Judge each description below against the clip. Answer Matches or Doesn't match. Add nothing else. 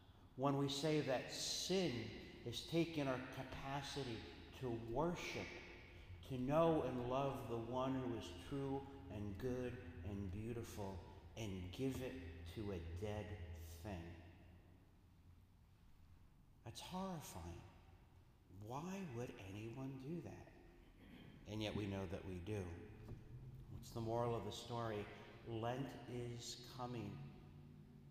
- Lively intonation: Matches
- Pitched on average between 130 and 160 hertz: Doesn't match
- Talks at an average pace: Doesn't match